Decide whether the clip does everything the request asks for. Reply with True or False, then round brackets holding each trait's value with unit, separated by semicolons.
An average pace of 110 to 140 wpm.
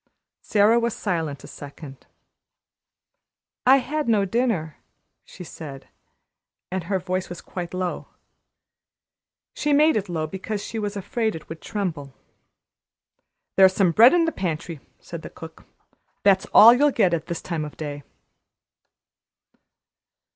True (135 wpm)